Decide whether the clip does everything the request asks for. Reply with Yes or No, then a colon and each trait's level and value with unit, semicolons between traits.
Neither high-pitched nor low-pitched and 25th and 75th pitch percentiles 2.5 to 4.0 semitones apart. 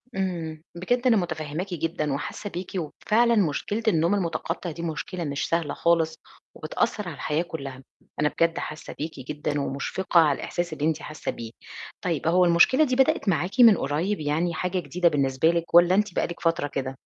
Yes: medium, 170 Hz; average, 3.3 semitones